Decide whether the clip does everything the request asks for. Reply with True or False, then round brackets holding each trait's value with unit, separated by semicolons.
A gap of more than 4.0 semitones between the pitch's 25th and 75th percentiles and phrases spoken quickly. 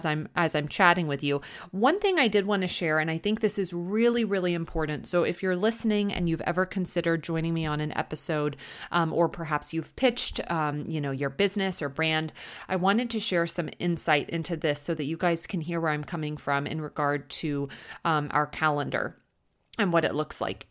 False (3.6 semitones; 220 wpm)